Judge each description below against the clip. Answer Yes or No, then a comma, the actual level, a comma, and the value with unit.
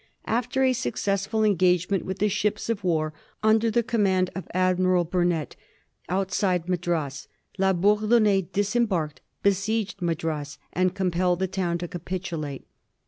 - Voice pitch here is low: No, medium, 185 Hz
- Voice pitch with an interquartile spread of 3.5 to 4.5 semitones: No, average, 2.9 semitones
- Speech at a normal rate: No, slow, 130 wpm